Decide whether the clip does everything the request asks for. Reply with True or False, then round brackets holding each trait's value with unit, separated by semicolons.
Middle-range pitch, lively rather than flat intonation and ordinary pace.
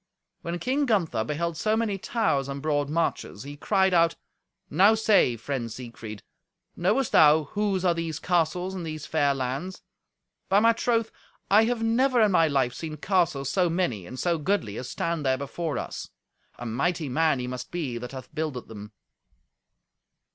True (160 Hz; 5.8 semitones; 170 wpm)